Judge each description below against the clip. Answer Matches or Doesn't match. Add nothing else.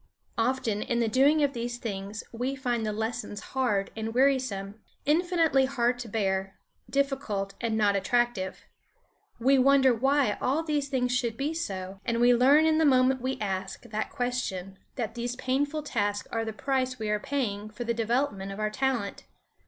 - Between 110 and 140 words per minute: Doesn't match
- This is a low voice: Doesn't match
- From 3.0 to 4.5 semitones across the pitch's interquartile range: Matches